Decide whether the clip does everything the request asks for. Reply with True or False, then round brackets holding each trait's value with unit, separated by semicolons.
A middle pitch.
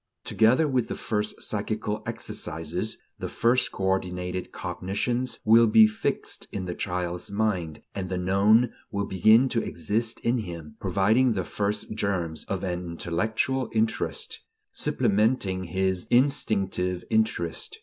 False (100 Hz)